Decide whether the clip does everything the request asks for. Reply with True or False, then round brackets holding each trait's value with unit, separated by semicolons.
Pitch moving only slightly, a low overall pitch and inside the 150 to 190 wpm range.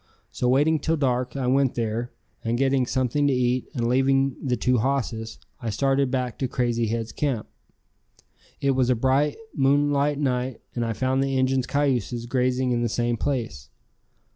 True (2.2 semitones; 130 Hz; 170 wpm)